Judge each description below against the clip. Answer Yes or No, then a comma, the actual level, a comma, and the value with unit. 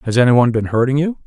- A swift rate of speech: Yes, fast, 235 wpm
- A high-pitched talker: No, low, 130 Hz